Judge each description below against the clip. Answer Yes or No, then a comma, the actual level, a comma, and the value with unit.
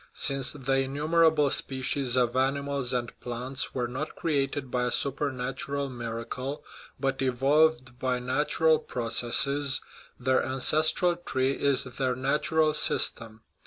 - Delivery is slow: Yes, slow, 125 wpm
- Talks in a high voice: No, low, 135 Hz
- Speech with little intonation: Yes, narrow, 2.3 semitones